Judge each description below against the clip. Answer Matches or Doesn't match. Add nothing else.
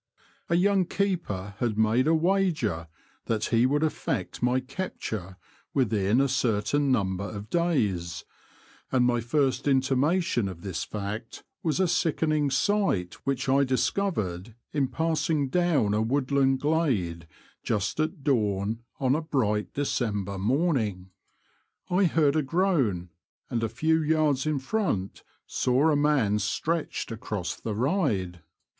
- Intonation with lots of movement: Matches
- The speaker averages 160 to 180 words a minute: Doesn't match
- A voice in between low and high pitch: Doesn't match